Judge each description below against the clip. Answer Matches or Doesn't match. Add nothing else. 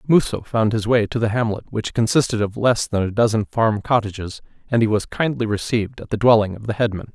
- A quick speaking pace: Matches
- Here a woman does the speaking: Doesn't match